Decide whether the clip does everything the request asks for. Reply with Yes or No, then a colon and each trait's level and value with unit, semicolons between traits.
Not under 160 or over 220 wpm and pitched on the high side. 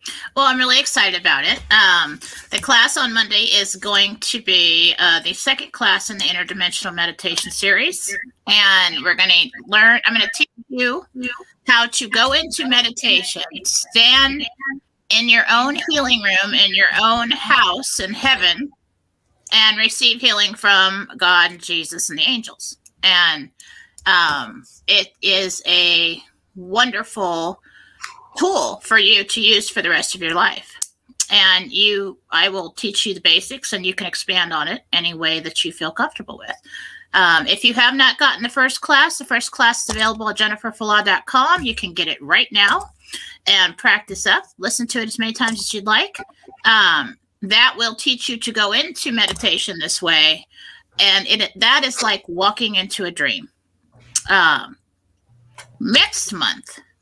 Yes: average, 165 wpm; high, 220 Hz